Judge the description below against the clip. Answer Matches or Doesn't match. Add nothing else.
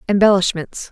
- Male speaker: Doesn't match